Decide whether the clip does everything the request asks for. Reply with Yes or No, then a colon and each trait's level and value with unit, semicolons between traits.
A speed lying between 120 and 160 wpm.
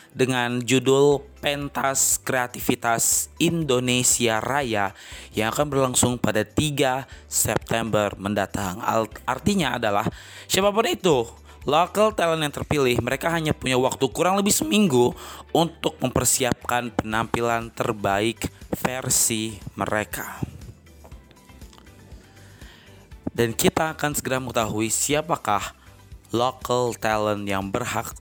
No: average, 95 wpm